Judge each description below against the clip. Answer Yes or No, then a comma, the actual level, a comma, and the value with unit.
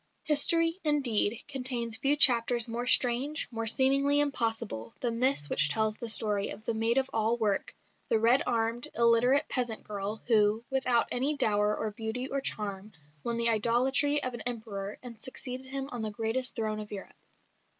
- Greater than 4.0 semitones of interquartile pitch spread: No, average, 3.2 semitones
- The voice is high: Yes, high, 235 Hz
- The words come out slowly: No, average, 170 wpm